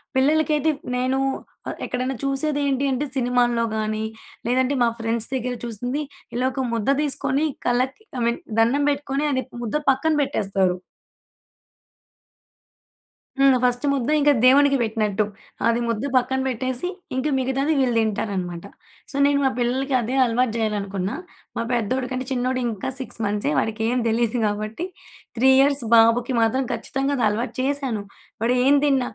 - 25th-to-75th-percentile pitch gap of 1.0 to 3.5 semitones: Yes, average, 3.1 semitones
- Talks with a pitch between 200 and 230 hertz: No, very high, 250 Hz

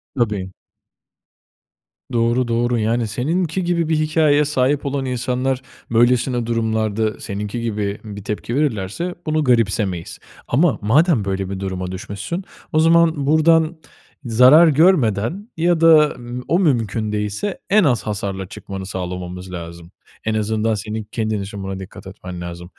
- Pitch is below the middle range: Yes, low, 115 Hz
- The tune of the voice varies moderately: No, wide, 7.1 semitones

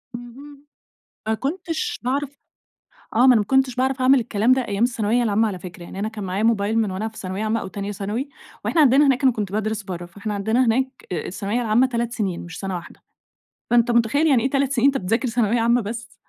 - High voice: Yes, high, 230 Hz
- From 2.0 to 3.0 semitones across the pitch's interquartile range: No, average, 3.9 semitones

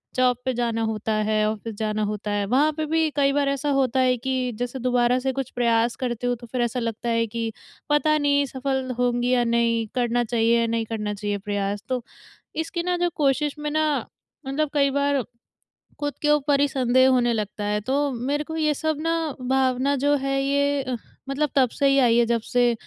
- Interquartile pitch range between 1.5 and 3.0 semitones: No, average, 3.5 semitones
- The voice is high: Yes, very high, 255 Hz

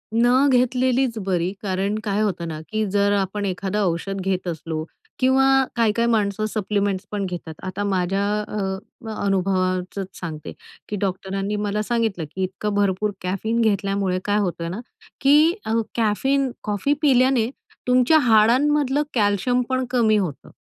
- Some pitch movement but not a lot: Yes, average, 3.8 semitones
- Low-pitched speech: No, high, 205 Hz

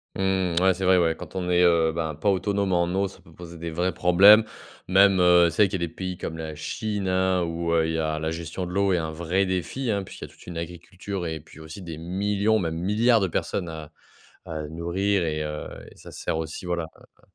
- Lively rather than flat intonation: No, average, 2.8 semitones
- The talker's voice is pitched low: Yes, very low, 90 Hz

